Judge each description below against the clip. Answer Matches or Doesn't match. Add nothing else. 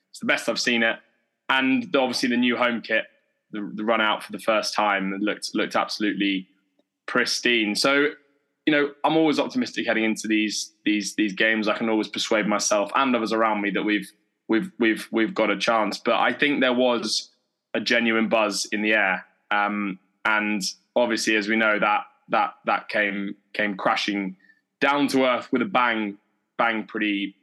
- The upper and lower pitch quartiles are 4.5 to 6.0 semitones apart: Doesn't match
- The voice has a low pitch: Matches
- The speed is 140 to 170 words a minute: Doesn't match